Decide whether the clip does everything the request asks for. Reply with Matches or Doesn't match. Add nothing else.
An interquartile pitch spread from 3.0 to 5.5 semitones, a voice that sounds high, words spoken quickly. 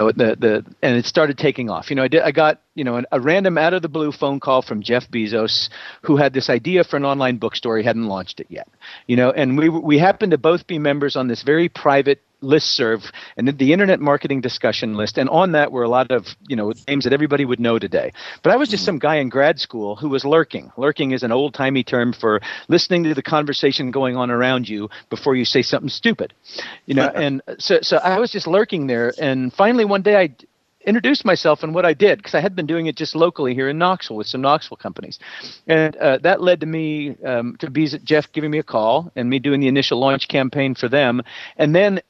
Doesn't match